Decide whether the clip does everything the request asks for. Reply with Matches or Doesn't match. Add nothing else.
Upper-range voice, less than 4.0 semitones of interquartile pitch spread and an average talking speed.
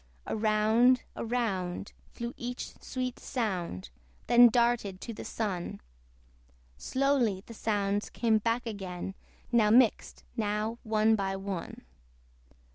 Doesn't match